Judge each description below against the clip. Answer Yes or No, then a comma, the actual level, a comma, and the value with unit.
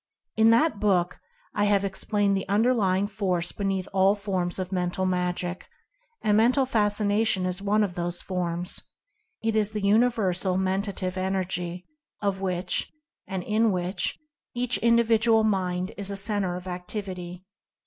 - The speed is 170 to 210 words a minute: No, average, 150 wpm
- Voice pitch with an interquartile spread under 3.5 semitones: Yes, average, 2.9 semitones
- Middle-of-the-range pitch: No, high, 195 Hz